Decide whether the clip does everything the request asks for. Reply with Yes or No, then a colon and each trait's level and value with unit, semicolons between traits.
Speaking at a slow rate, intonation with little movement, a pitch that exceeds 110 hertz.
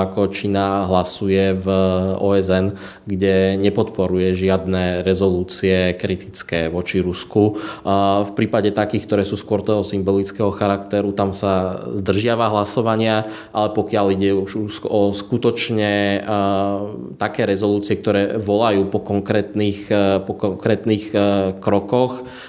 No: slow, 105 wpm; narrow, 1.6 semitones; low, 100 Hz